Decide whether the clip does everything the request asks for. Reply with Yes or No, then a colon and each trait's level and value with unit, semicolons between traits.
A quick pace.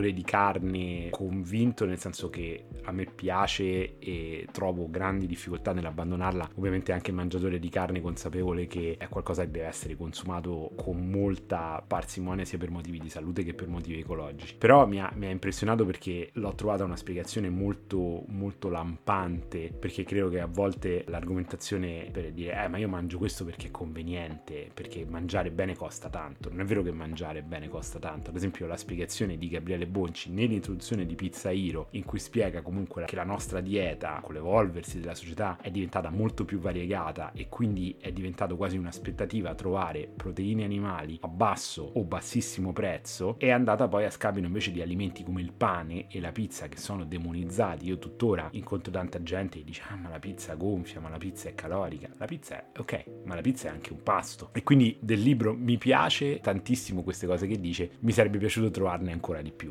Yes: fast, 190 wpm